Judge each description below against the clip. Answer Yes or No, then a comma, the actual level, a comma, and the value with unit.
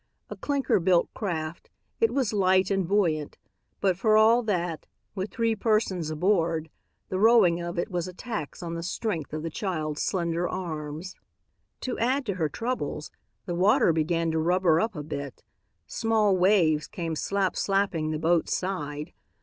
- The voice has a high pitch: No, medium, 180 Hz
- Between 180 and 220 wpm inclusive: No, average, 165 wpm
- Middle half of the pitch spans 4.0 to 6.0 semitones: Yes, average, 4.3 semitones